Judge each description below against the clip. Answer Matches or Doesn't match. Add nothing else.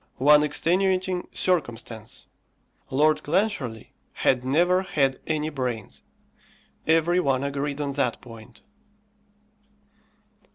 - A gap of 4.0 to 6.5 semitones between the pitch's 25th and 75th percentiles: Matches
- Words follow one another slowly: Matches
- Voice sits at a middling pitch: Matches